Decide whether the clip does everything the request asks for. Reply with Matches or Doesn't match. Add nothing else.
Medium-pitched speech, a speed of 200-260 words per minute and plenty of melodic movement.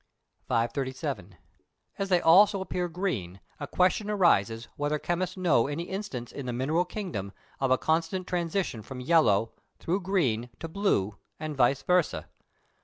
Doesn't match